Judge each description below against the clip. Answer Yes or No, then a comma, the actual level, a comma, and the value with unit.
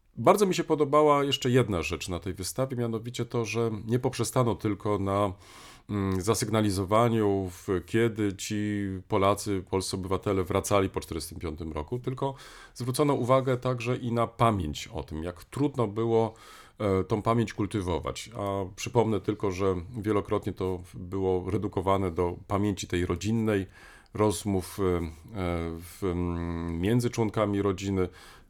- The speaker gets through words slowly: No, average, 120 wpm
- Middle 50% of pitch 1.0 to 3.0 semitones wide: No, average, 3.7 semitones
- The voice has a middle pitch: No, low, 105 Hz